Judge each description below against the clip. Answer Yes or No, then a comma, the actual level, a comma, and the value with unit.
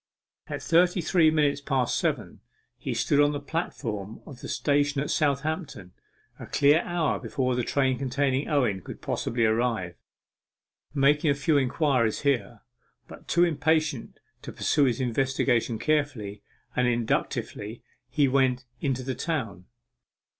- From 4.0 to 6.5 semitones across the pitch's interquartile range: No, average, 3.5 semitones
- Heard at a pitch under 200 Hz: Yes, low, 135 Hz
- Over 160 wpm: No, average, 140 wpm